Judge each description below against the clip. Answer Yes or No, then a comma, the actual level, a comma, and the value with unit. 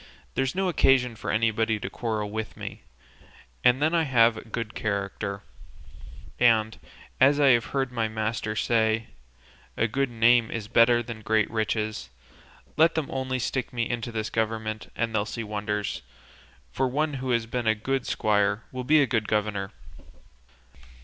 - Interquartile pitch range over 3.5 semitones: No, average, 2.8 semitones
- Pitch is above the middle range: No, low, 115 Hz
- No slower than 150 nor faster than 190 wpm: Yes, average, 165 wpm